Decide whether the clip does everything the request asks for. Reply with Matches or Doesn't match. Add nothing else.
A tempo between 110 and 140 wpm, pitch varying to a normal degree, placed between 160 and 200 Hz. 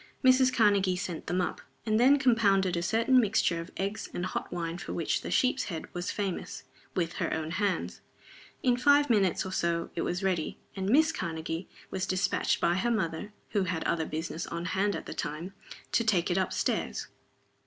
Doesn't match